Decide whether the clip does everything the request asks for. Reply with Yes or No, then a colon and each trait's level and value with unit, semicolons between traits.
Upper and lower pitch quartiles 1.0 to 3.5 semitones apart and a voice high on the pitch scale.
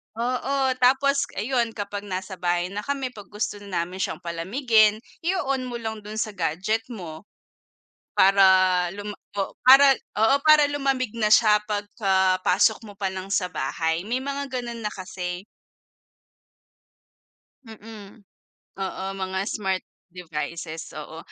No: average, 4.3 semitones; high, 210 Hz